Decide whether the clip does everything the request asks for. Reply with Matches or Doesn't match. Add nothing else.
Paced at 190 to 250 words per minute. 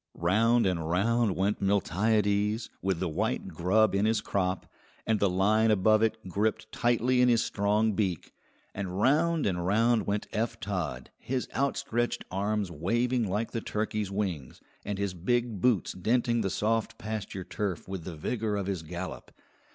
Doesn't match